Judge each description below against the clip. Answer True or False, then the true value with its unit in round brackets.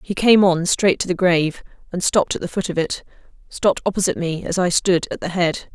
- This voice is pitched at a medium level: True (180 Hz)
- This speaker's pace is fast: True (230 wpm)